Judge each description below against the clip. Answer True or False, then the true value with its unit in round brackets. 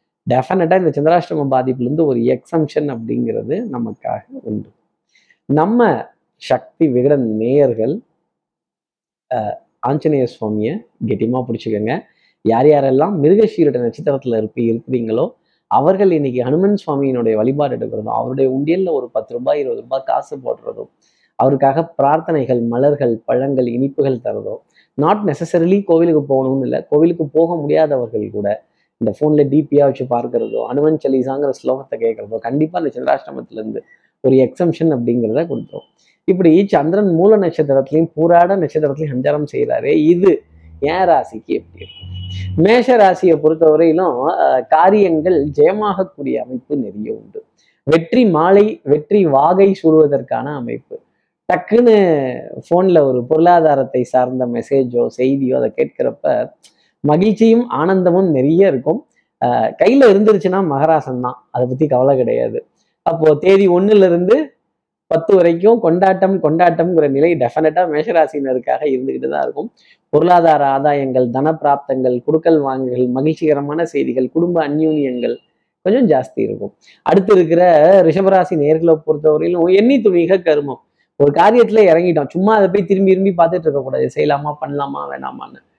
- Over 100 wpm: True (110 wpm)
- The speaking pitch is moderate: True (155 Hz)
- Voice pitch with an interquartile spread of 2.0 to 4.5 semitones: False (5.4 semitones)